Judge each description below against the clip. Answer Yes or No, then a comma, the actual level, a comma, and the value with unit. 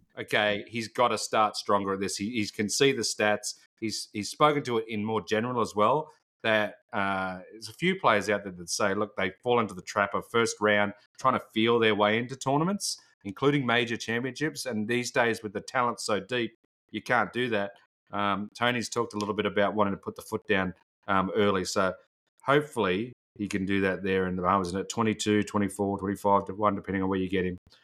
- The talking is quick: Yes, fast, 220 wpm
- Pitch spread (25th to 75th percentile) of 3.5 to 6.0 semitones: No, average, 2.8 semitones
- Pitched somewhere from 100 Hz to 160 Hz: Yes, low, 105 Hz